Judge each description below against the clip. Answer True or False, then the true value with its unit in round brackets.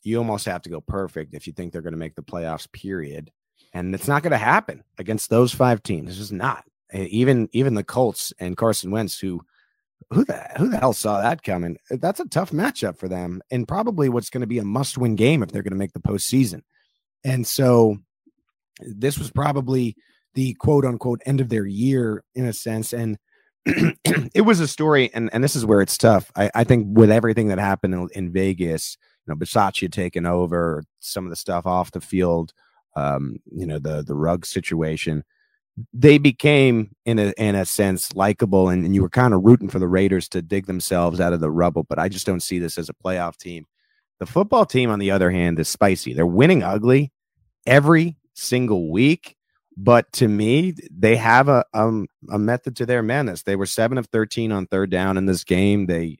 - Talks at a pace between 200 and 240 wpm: True (205 wpm)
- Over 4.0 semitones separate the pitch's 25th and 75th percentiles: True (5.4 semitones)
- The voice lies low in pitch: True (105 Hz)